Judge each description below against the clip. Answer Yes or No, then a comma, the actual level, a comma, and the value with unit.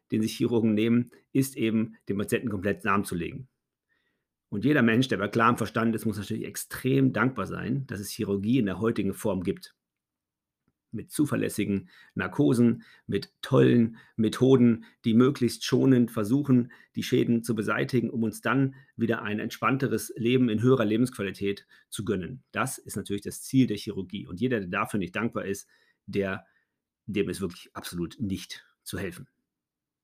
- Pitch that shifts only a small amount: No, average, 3.4 semitones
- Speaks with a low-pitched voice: Yes, low, 115 Hz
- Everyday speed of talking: Yes, average, 160 wpm